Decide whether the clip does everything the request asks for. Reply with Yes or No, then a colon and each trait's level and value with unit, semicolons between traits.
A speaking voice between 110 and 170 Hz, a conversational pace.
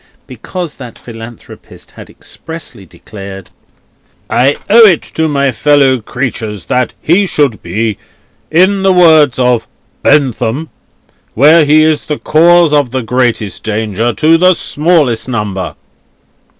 No: medium, 140 Hz; slow, 125 wpm